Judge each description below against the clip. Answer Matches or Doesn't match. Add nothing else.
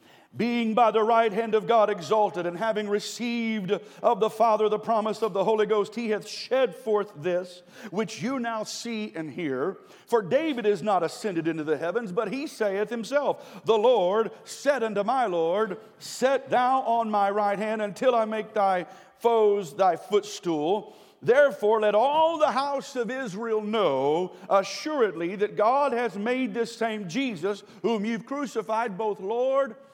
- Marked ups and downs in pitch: Doesn't match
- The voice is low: Doesn't match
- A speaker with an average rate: Matches